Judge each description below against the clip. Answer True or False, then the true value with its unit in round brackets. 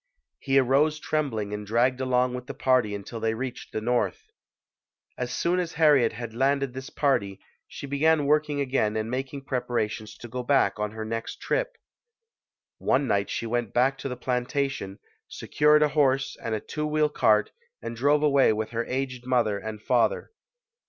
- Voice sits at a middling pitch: False (125 Hz)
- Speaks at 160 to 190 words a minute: True (175 wpm)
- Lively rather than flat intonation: False (3.9 semitones)